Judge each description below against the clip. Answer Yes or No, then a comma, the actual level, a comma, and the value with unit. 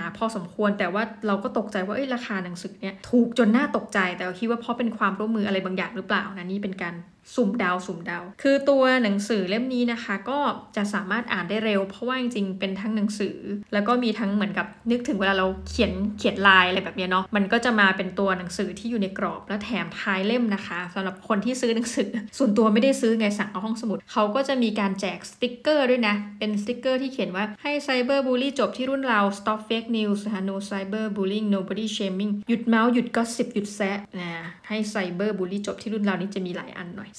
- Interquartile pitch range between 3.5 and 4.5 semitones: No, average, 3.1 semitones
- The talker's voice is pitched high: Yes, high, 210 Hz